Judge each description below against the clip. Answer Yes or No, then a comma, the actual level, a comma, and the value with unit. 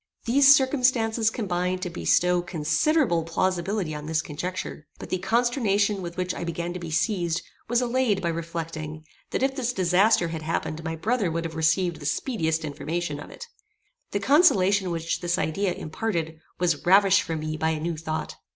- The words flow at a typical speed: Yes, average, 175 wpm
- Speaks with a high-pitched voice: No, medium, 175 Hz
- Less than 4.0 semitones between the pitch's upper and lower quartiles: No, average, 4.5 semitones